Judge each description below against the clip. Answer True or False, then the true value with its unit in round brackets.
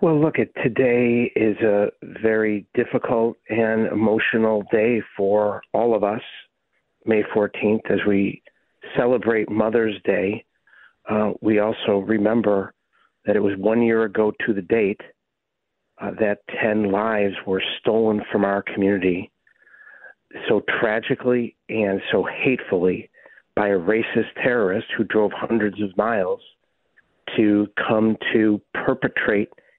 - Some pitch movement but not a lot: False (1.6 semitones)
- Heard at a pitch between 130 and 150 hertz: False (110 Hz)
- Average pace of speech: False (125 wpm)